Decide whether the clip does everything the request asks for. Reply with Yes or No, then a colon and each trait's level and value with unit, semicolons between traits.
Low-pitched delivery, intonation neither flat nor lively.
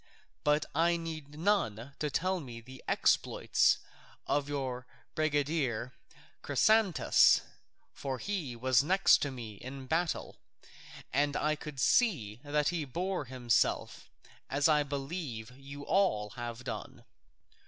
No: medium, 145 Hz; average, 4.2 semitones